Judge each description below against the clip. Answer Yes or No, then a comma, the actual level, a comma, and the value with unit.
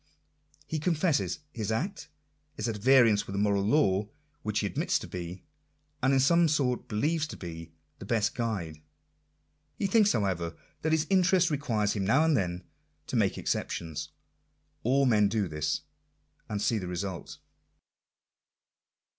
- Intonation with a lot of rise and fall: Yes, wide, 7.4 semitones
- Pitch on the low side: Yes, low, 110 Hz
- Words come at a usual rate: Yes, average, 160 wpm